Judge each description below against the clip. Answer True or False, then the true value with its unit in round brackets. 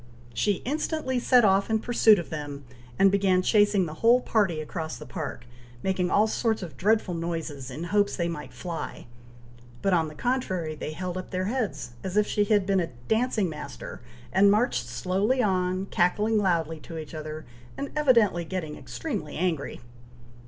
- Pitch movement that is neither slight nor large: True (4.8 semitones)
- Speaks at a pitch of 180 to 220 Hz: True (185 Hz)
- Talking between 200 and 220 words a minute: False (175 wpm)